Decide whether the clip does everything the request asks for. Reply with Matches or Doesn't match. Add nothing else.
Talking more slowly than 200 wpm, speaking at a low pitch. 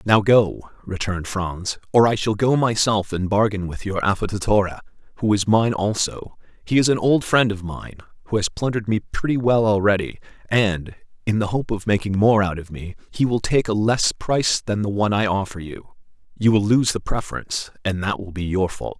Doesn't match